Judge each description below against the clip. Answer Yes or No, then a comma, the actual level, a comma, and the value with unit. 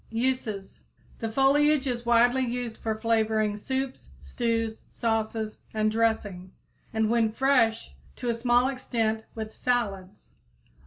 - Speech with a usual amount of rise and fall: No, narrow, 2.1 semitones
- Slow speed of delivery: Yes, slow, 120 wpm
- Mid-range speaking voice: No, high, 230 Hz